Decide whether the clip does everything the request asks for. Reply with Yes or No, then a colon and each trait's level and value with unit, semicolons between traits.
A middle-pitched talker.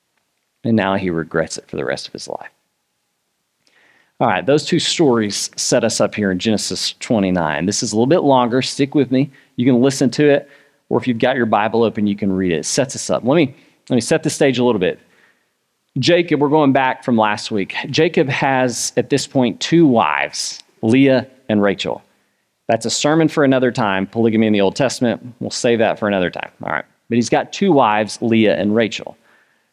No: low, 125 Hz